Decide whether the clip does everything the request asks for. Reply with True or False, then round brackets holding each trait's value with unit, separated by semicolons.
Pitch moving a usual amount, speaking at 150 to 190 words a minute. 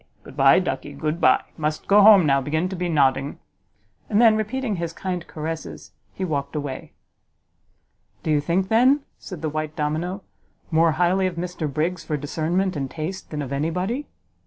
True (3.8 semitones; 180 wpm)